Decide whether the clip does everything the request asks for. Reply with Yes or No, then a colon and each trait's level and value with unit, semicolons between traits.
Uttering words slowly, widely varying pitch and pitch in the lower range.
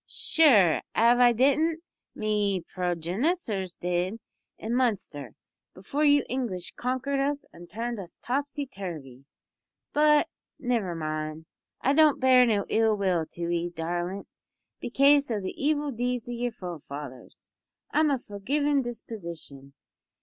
No: slow, 130 wpm; wide, 7.6 semitones; high, 220 Hz